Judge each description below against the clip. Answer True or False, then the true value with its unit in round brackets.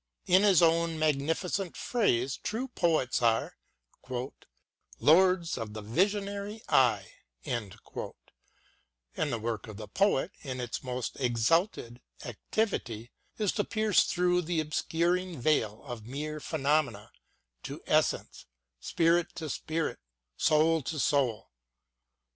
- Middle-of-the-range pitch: True (155 Hz)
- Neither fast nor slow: False (115 wpm)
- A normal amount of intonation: False (6.8 semitones)